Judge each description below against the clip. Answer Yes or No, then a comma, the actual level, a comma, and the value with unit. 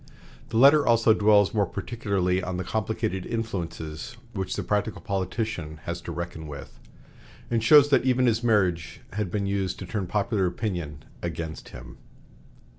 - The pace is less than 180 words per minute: Yes, average, 155 wpm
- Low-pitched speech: Yes, low, 100 Hz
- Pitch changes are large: No, average, 4.5 semitones